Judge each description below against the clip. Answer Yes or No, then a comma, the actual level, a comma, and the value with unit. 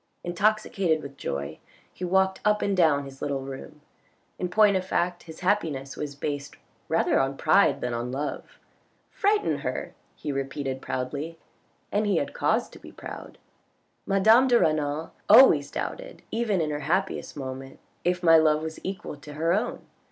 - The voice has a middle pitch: Yes, medium, 160 Hz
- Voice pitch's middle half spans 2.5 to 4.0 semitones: No, wide, 5.4 semitones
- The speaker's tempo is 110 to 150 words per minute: No, average, 175 wpm